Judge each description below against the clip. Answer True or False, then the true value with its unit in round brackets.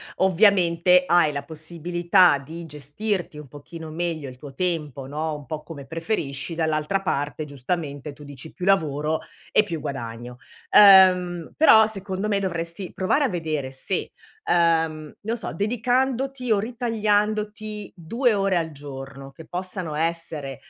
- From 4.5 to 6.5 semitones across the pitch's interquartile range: True (4.8 semitones)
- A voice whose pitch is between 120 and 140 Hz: False (170 Hz)